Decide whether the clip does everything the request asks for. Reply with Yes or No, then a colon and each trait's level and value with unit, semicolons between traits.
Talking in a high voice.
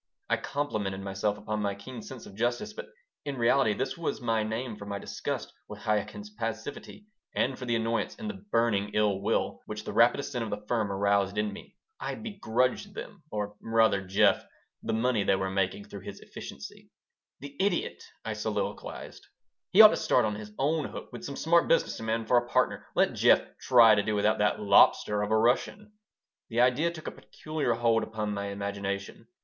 No: low, 110 Hz